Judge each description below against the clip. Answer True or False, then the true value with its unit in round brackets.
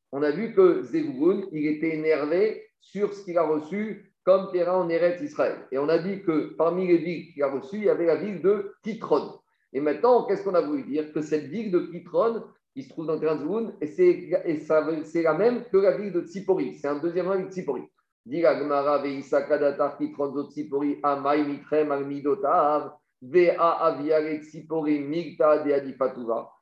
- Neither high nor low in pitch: True (165 Hz)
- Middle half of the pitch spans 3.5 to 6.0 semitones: True (4.5 semitones)